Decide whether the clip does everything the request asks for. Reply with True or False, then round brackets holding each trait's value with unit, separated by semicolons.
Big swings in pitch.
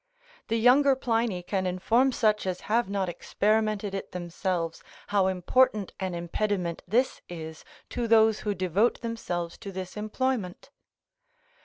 False (4.0 semitones)